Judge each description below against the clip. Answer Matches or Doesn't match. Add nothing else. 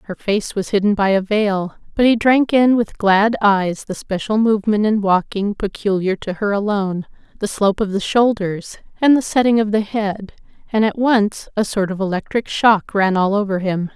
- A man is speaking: Doesn't match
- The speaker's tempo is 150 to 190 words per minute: Doesn't match